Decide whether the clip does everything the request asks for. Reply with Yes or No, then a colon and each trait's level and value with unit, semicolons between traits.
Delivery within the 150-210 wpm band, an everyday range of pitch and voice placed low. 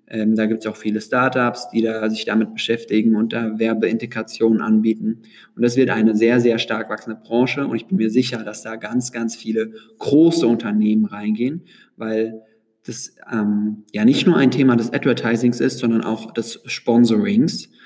No: average, 180 wpm; narrow, 1.6 semitones; low, 115 Hz